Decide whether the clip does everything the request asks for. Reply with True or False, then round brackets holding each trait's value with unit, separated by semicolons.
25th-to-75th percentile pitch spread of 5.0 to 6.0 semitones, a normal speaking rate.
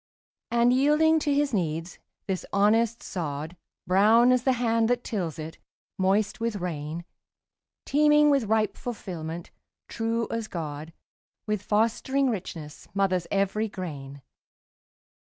False (5.5 semitones; 120 wpm)